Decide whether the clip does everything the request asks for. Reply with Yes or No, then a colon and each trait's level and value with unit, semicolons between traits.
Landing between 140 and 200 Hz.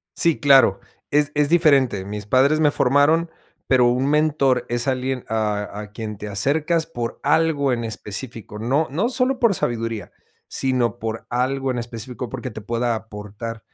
No: low, 125 Hz